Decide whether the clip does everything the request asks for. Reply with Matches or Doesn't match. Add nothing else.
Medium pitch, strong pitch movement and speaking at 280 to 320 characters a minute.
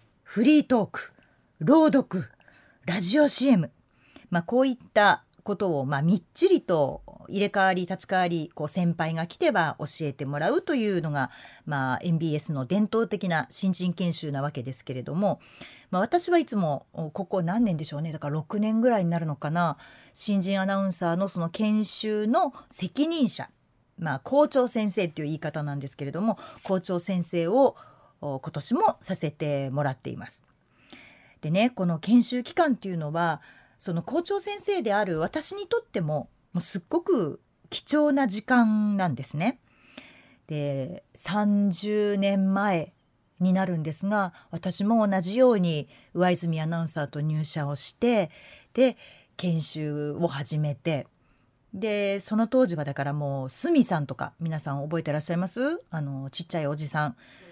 Matches